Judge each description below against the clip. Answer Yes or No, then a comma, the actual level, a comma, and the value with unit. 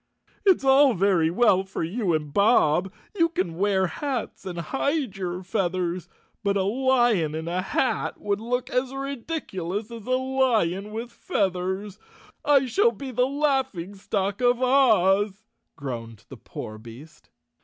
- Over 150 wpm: No, average, 145 wpm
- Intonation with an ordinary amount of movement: No, wide, 6.2 semitones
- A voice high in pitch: Yes, high, 205 Hz